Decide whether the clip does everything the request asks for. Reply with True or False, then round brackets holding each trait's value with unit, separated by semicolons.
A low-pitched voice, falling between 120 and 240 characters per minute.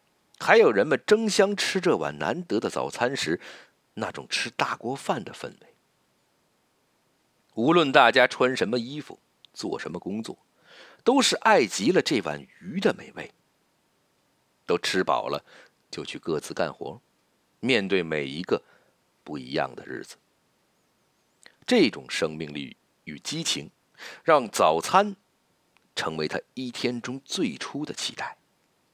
True (125 Hz; 190 characters per minute)